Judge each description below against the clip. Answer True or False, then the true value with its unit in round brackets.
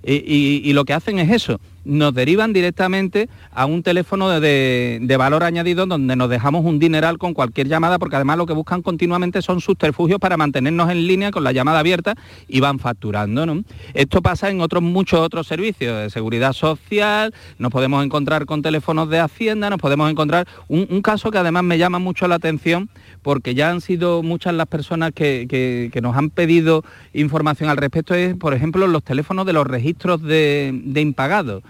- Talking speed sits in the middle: False (195 wpm)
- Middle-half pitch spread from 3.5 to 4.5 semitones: True (4.1 semitones)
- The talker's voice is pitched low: False (160 Hz)